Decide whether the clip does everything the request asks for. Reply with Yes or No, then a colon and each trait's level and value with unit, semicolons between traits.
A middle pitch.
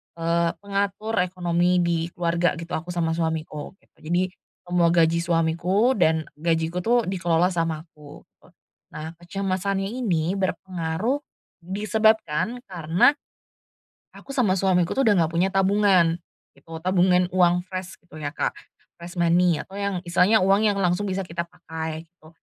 Yes: medium, 175 Hz